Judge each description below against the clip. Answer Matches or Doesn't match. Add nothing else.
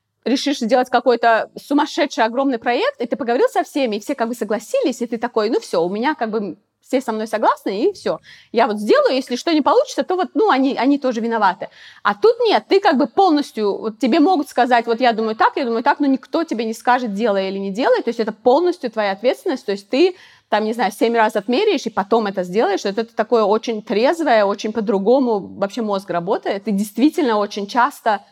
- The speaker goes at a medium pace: Doesn't match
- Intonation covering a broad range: Doesn't match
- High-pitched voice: Matches